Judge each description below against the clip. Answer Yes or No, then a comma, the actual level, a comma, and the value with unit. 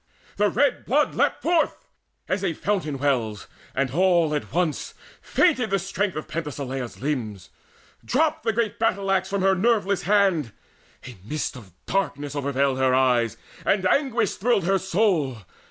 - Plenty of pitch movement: Yes, wide, 7.0 semitones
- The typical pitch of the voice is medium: Yes, medium, 180 Hz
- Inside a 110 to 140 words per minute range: No, average, 155 wpm